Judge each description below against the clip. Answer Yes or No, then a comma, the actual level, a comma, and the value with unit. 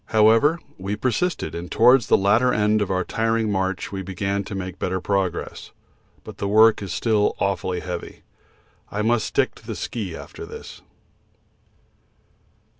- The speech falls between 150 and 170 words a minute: Yes, average, 155 wpm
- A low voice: Yes, low, 100 Hz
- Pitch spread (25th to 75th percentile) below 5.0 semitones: Yes, average, 3.0 semitones